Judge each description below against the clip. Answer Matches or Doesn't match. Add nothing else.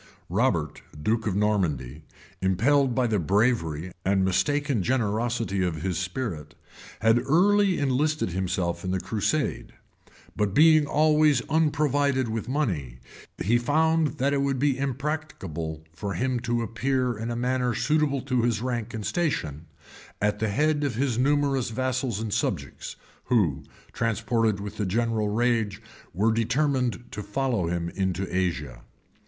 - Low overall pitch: Matches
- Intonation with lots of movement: Matches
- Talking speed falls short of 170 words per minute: Matches